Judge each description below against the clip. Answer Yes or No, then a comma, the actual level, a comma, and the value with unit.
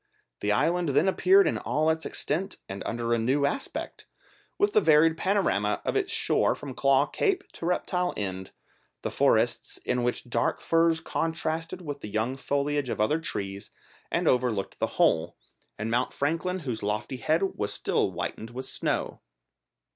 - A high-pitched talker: No, medium, 140 Hz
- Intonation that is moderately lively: No, wide, 6.0 semitones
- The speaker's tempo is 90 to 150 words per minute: No, average, 165 wpm